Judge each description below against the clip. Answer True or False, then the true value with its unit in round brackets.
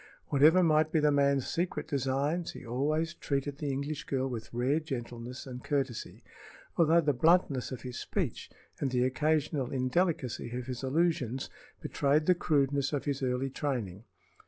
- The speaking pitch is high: False (140 Hz)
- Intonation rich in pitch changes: False (3.2 semitones)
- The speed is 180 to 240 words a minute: False (160 wpm)